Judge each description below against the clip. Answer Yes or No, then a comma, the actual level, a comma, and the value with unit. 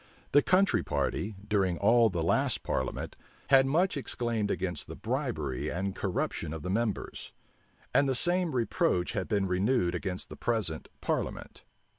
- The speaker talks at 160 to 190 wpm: No, average, 150 wpm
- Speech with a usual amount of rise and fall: No, wide, 6.5 semitones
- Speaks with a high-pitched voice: No, low, 105 Hz